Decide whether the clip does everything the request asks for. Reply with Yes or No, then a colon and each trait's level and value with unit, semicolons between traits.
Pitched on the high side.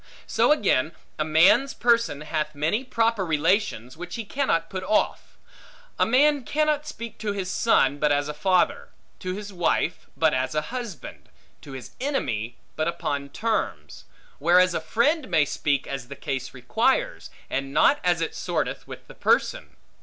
No: medium, 175 Hz